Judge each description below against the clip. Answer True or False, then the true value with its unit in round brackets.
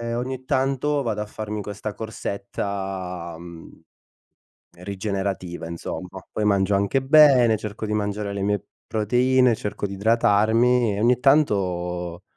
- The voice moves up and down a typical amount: True (3.6 semitones)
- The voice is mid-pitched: False (105 Hz)